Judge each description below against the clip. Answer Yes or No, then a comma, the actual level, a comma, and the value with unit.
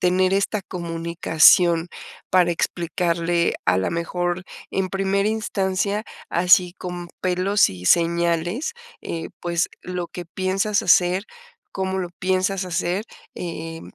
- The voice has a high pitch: No, medium, 180 Hz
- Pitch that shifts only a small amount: Yes, narrow, 2.0 semitones